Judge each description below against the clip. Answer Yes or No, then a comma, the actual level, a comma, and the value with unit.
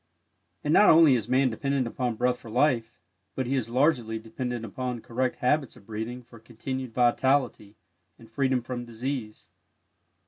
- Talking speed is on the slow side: No, average, 160 wpm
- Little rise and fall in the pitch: Yes, narrow, 2.3 semitones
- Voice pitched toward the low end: Yes, low, 125 Hz